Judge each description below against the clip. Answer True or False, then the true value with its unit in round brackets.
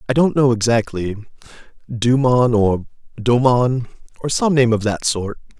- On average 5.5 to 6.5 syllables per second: False (4.4 syllables/s)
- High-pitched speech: False (120 Hz)